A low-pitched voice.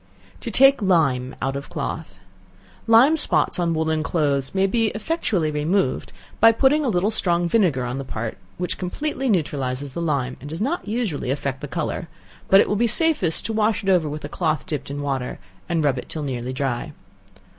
No: medium, 165 Hz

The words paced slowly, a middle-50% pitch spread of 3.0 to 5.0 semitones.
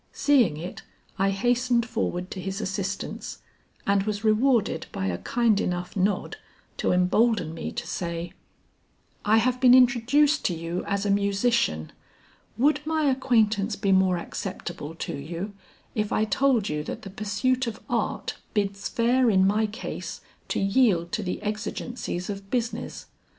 No: average, 150 wpm; average, 4.2 semitones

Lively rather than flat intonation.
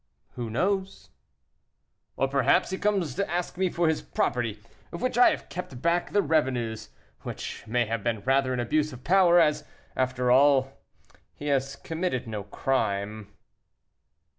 Yes: wide, 6.2 semitones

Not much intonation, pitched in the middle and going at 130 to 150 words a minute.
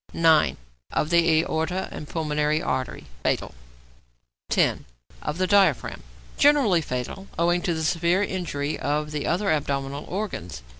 No: average, 3.2 semitones; medium, 160 Hz; slow, 135 wpm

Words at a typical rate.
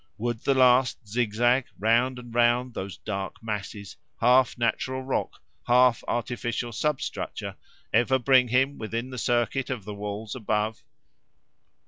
No: slow, 130 wpm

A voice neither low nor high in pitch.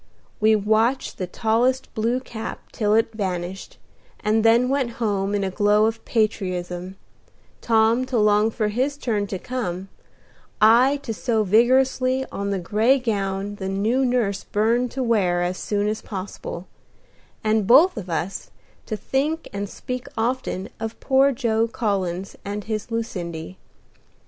No: high, 220 Hz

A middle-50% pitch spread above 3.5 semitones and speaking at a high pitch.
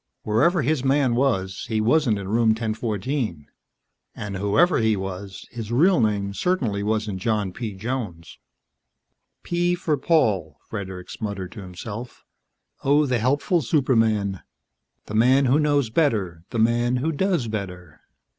No: average, 5.3 semitones; low, 110 Hz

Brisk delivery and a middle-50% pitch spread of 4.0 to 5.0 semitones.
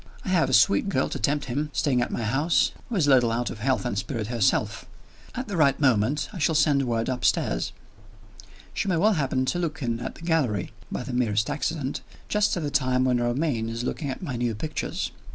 Yes: fast, 225 wpm; average, 4.5 semitones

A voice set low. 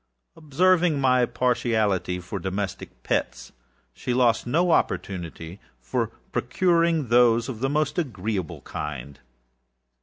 Yes: low, 120 Hz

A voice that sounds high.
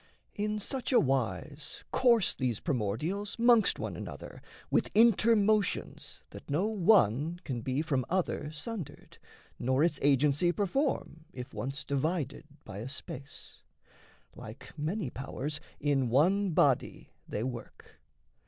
No: medium, 150 Hz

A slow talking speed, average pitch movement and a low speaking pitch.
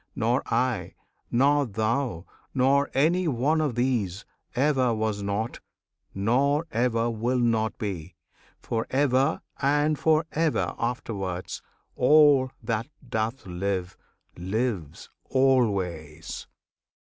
Yes: slow, 100 wpm; average, 4.8 semitones; low, 120 Hz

